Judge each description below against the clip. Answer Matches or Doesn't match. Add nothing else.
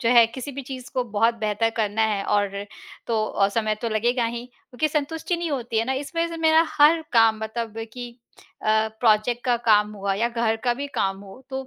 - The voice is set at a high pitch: Matches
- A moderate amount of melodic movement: Matches